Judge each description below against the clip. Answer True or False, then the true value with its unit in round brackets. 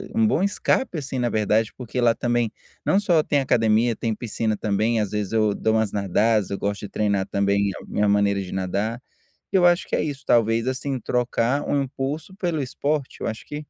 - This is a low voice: True (115 Hz)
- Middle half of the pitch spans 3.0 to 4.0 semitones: False (4.9 semitones)